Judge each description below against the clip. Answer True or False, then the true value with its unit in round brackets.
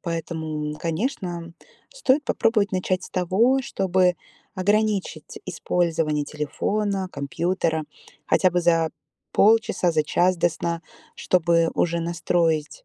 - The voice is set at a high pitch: False (175 Hz)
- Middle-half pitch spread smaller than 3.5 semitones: True (2.9 semitones)